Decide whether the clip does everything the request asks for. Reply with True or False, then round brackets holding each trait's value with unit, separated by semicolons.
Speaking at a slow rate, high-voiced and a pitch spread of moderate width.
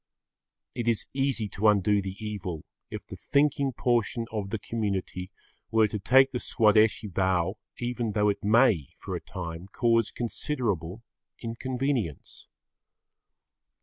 False (130 wpm; 110 Hz; 3.6 semitones)